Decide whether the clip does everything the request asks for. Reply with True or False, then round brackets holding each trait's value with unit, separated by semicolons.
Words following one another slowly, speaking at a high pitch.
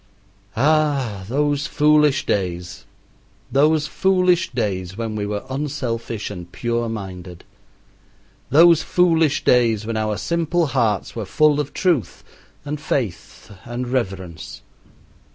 False (115 wpm; 125 Hz)